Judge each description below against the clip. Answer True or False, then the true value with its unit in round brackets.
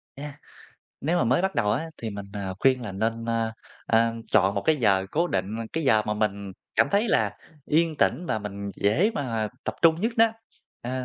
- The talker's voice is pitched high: False (115 Hz)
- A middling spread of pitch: False (7.3 semitones)